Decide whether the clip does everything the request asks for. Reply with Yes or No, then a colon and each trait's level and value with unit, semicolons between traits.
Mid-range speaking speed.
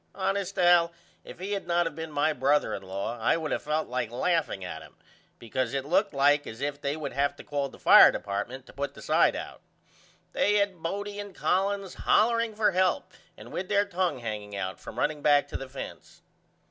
No: fast, 210 wpm